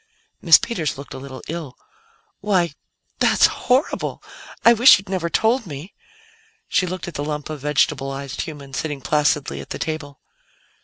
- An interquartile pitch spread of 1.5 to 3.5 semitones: No, average, 4.7 semitones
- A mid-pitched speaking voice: Yes, medium, 155 Hz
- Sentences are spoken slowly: No, average, 155 wpm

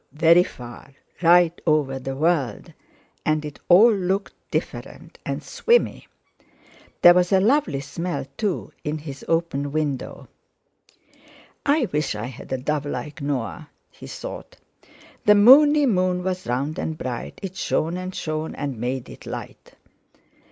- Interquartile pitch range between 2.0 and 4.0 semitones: No, average, 4.8 semitones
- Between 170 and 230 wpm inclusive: No, average, 140 wpm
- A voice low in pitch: No, medium, 155 Hz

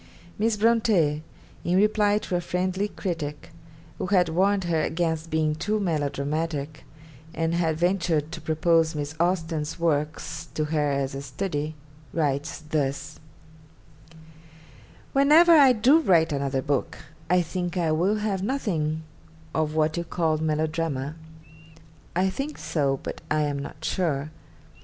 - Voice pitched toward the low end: No, medium, 160 Hz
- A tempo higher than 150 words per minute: No, slow, 135 wpm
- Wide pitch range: No, average, 3.6 semitones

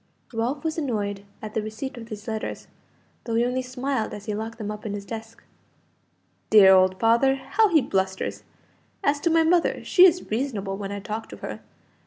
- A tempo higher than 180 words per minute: Yes, average, 195 wpm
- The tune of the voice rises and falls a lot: No, average, 4.5 semitones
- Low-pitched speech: No, high, 225 Hz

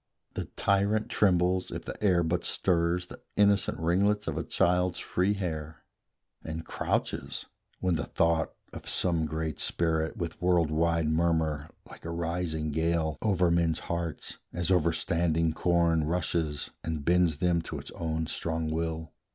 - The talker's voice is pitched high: No, very low, 85 Hz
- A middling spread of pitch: No, narrow, 1.9 semitones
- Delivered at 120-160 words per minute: Yes, average, 150 wpm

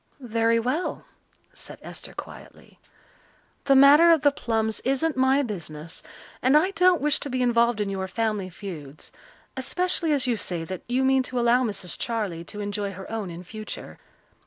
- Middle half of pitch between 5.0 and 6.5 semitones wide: Yes, wide, 5.4 semitones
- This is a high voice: Yes, high, 235 Hz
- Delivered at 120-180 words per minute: Yes, average, 170 wpm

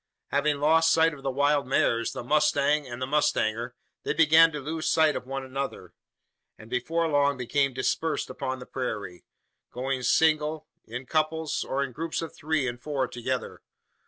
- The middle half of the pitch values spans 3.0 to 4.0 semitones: Yes, average, 3.3 semitones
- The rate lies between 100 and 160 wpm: No, average, 170 wpm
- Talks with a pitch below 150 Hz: Yes, medium, 140 Hz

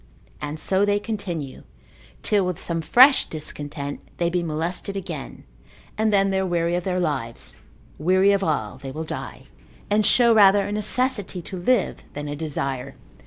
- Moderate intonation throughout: Yes, average, 4.7 semitones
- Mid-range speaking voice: Yes, medium, 180 Hz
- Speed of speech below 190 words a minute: Yes, average, 165 wpm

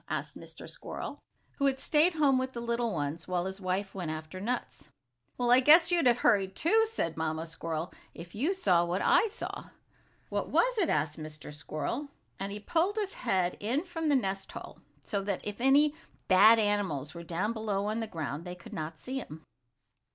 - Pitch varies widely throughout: Yes, wide, 7.9 semitones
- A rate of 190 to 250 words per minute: Yes, average, 200 wpm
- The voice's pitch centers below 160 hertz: No, high, 205 Hz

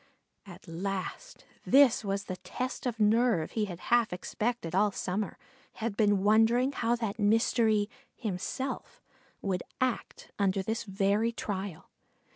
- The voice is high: Yes, high, 210 Hz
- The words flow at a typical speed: No, slow, 130 wpm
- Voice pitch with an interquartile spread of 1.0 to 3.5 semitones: Yes, average, 3.1 semitones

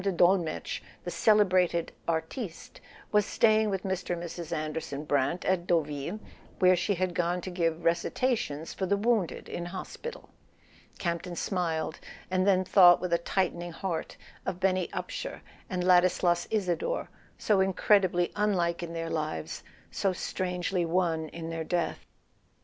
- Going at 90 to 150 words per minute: Yes, average, 145 wpm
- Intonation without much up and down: Yes, narrow, 2.2 semitones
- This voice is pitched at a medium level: Yes, medium, 175 Hz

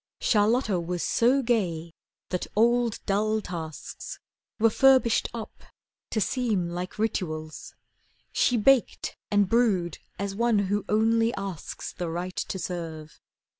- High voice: Yes, high, 205 Hz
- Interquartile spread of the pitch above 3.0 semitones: Yes, average, 4.5 semitones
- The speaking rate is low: Yes, slow, 125 wpm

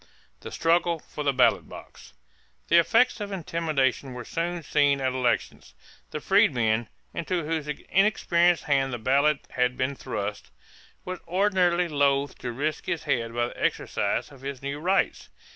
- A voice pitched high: No, medium, 145 Hz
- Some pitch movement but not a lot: Yes, average, 4.8 semitones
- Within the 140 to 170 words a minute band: Yes, average, 155 wpm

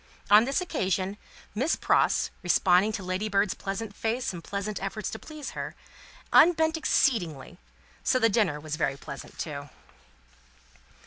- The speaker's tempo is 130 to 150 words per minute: Yes, slow, 135 wpm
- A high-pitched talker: Yes, high, 200 Hz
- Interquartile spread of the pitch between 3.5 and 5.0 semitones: Yes, average, 4.6 semitones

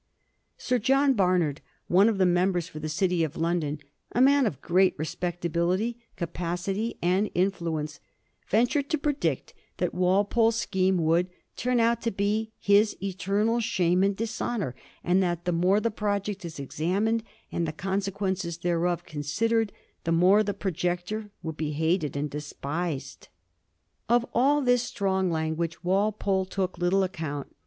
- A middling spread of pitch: Yes, average, 3.8 semitones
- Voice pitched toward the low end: No, medium, 185 Hz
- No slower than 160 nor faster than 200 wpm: No, average, 145 wpm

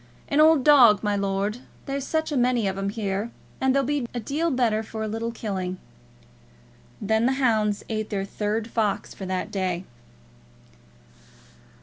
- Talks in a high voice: Yes, high, 220 Hz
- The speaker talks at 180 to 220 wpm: No, average, 160 wpm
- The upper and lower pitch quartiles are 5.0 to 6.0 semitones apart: No, average, 4.4 semitones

